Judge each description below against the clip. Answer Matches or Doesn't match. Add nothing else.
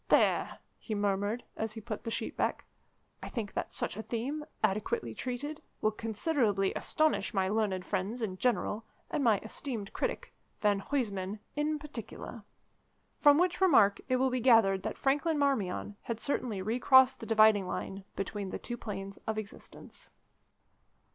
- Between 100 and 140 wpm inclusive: Doesn't match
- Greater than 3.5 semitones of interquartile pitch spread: Matches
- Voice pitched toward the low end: Doesn't match